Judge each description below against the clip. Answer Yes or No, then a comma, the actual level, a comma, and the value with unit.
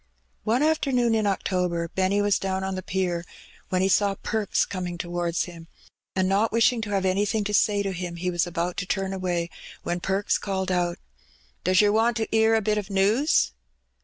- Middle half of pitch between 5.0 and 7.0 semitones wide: No, average, 2.8 semitones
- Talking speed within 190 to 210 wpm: Yes, average, 200 wpm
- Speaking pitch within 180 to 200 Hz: Yes, high, 190 Hz